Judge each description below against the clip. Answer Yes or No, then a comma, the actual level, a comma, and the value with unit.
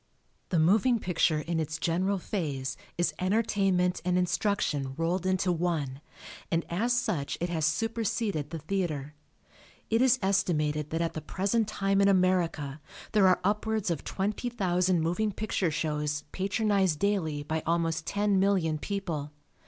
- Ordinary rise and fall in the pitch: Yes, average, 4.1 semitones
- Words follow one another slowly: No, average, 145 wpm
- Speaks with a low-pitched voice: No, medium, 180 Hz